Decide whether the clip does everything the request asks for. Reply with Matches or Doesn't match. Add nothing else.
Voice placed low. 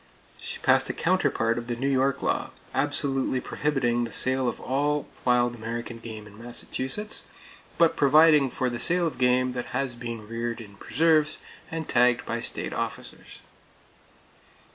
Matches